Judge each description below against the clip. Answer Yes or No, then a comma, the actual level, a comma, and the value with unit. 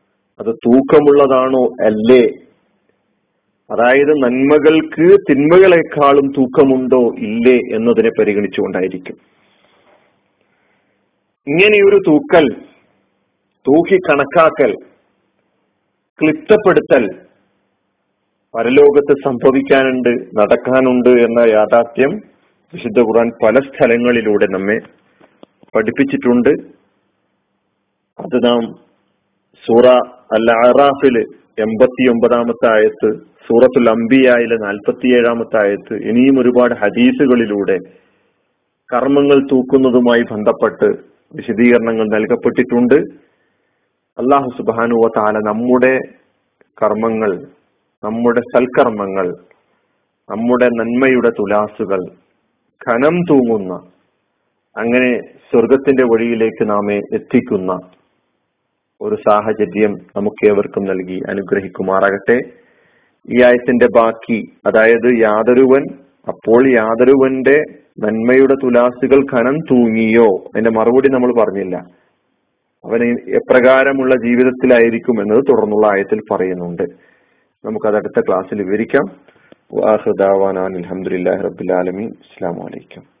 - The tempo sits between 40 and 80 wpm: Yes, average, 70 wpm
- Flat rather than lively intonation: No, average, 3.0 semitones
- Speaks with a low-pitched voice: Yes, low, 120 Hz